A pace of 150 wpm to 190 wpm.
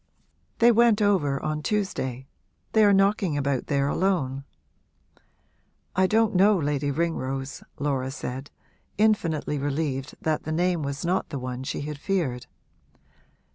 No: slow, 135 wpm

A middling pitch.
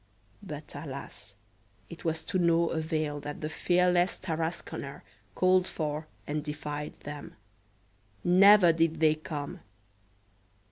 Yes: medium, 160 Hz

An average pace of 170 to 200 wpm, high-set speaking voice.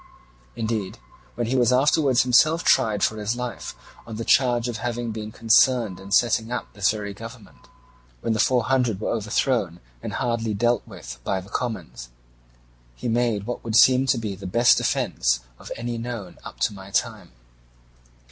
No: average, 175 wpm; low, 115 Hz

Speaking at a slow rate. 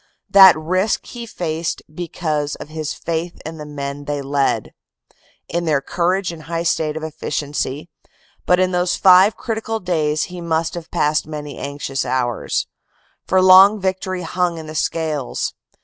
No: average, 155 wpm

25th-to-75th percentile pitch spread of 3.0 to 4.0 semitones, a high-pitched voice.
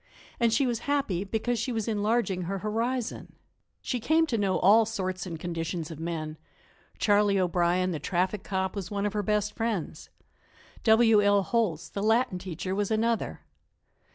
Yes: average, 3.6 semitones; high, 205 Hz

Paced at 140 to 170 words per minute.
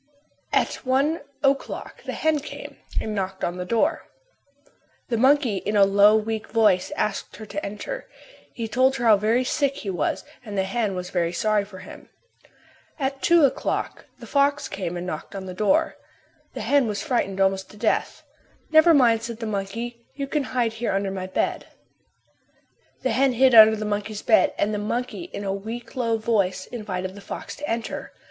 No: average, 185 wpm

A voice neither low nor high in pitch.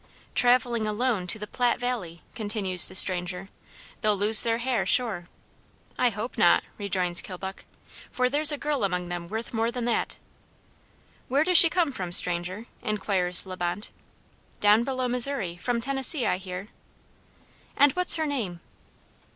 No: high, 215 Hz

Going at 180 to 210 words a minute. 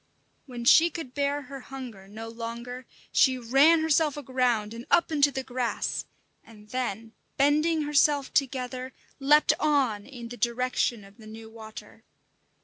No: average, 145 wpm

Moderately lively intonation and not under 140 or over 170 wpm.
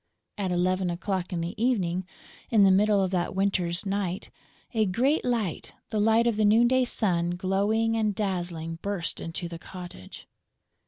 Yes: average, 3.4 semitones; average, 165 wpm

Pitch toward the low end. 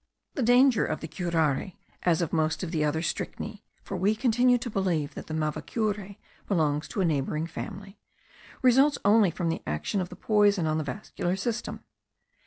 No: medium, 185 Hz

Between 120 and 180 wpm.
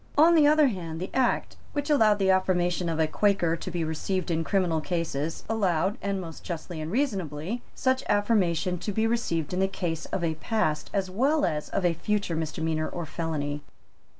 No: average, 190 wpm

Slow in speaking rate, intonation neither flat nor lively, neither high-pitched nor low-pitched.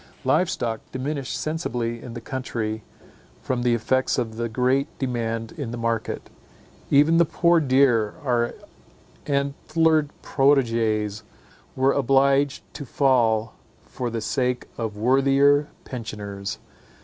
No: slow, 120 wpm; average, 3.4 semitones; low, 125 Hz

